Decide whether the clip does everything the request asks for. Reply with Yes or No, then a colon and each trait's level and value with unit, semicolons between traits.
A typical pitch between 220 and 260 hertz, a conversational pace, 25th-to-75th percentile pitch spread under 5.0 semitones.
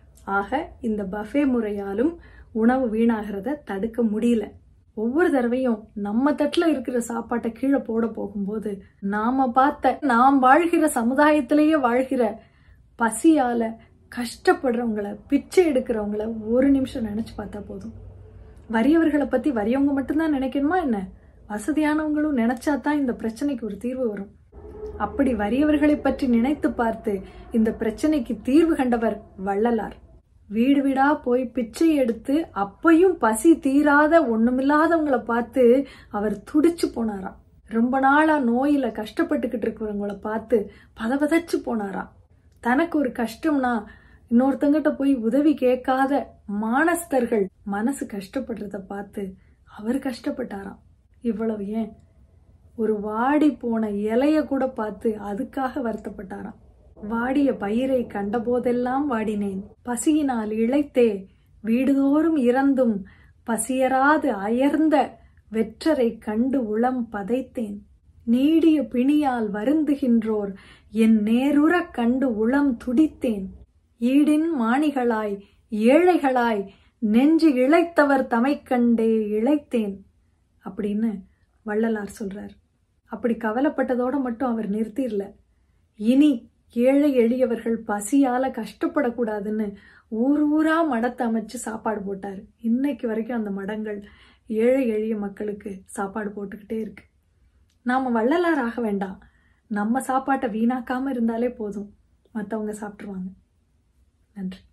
Yes: high, 240 Hz; average, 95 wpm; average, 4.2 semitones